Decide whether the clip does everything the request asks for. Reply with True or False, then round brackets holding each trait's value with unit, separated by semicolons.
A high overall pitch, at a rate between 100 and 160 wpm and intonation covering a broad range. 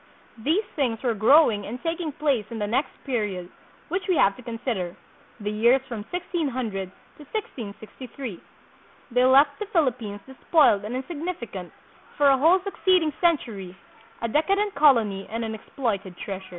True (250 Hz; 150 wpm; 6.5 semitones)